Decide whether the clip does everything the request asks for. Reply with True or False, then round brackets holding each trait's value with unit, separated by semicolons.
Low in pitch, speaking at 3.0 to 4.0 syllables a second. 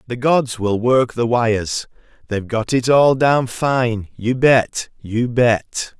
True (120 Hz; 3.5 syllables/s)